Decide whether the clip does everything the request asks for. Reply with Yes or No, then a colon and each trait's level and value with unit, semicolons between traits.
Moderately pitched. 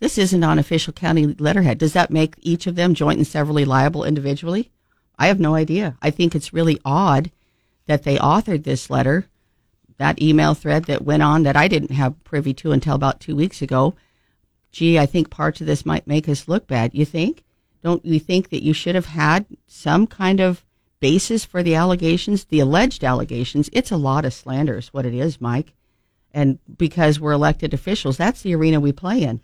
Yes: medium, 155 Hz